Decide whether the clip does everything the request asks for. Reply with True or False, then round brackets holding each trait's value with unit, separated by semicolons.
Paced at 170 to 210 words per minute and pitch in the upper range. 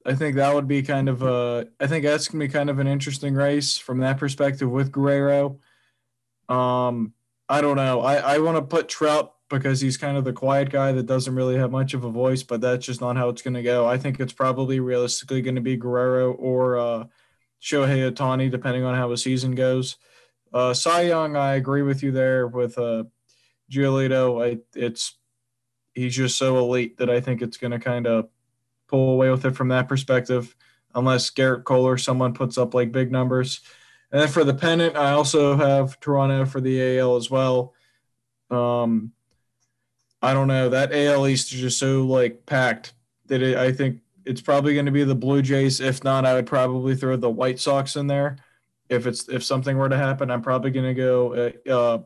False (200 wpm; 130 Hz)